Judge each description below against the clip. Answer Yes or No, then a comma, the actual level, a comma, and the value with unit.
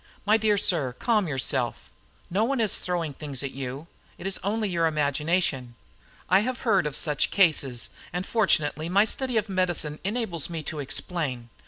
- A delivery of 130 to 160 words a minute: No, average, 170 wpm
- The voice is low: No, medium, 170 Hz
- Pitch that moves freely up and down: Yes, wide, 5.8 semitones